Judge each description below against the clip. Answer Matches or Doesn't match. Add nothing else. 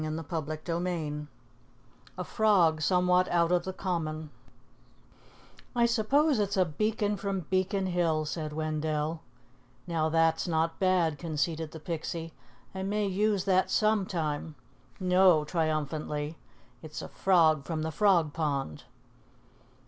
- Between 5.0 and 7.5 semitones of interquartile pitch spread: Doesn't match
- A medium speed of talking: Doesn't match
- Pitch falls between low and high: Matches